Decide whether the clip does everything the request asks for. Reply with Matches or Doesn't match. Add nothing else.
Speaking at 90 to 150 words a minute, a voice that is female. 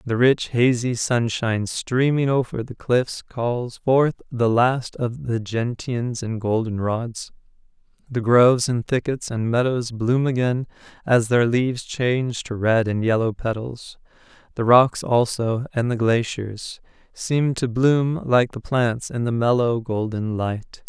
Doesn't match